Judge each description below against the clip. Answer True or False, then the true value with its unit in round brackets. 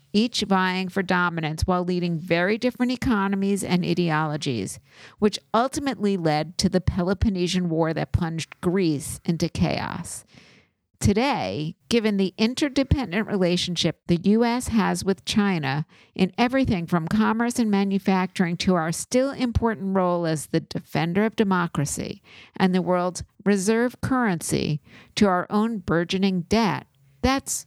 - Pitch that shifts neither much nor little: True (4.2 semitones)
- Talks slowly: True (130 wpm)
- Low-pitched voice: False (185 Hz)